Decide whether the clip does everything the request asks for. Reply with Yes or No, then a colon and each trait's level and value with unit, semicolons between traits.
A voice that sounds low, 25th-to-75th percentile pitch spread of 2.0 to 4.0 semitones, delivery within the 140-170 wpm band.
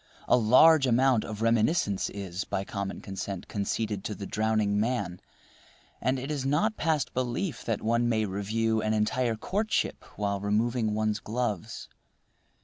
Yes: low, 110 Hz; average, 3.6 semitones; average, 145 wpm